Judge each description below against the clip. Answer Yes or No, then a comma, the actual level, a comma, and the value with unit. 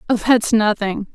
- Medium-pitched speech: No, high, 220 Hz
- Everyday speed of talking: Yes, average, 160 wpm